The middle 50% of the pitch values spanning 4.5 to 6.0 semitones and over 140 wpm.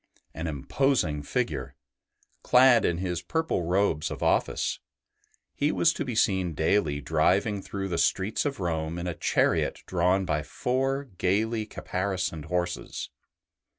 No: average, 5.1 semitones; slow, 135 wpm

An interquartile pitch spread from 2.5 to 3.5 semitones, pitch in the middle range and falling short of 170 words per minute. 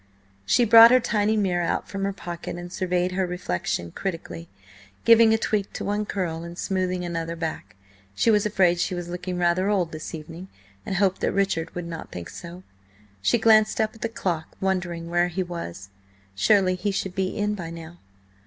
No: average, 3.0 semitones; medium, 180 Hz; average, 190 wpm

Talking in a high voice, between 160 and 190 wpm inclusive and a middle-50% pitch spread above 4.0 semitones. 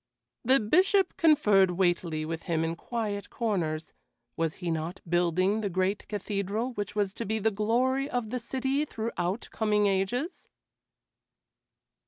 No: high, 205 Hz; average, 140 wpm; average, 4.8 semitones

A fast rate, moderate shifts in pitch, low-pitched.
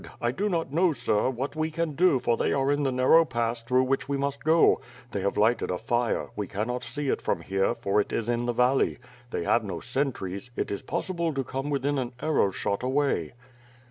Yes: fast, 225 wpm; average, 3.8 semitones; low, 130 Hz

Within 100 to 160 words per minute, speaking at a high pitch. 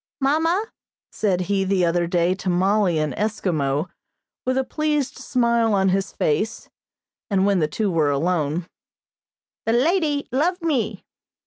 Yes: average, 140 wpm; high, 200 Hz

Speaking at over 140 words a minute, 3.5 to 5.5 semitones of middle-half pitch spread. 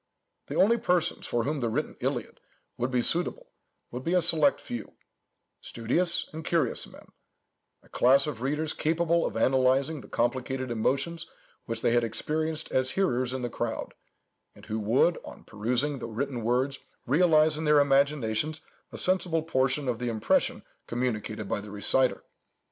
Yes: average, 160 wpm; average, 4.7 semitones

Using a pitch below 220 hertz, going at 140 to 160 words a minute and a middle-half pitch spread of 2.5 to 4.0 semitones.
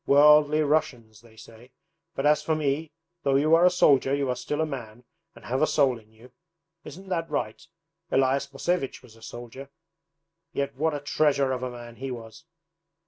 No: medium, 140 Hz; average, 190 wpm; average, 3.6 semitones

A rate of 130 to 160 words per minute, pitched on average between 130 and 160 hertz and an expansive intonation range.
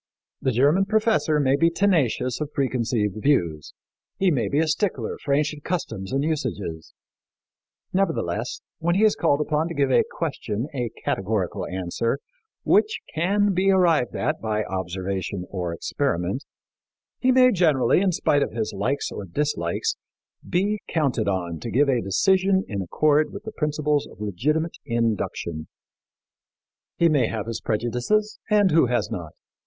Yes: average, 150 wpm; medium, 140 Hz; wide, 7.9 semitones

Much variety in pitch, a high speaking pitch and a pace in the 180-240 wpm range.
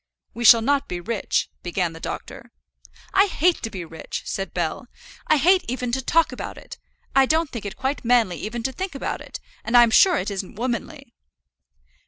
Yes: wide, 5.8 semitones; high, 240 Hz; average, 200 wpm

